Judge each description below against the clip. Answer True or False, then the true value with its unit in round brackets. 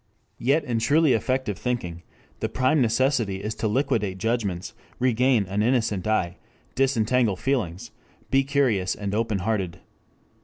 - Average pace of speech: False (130 wpm)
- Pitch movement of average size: True (4.4 semitones)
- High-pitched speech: False (115 Hz)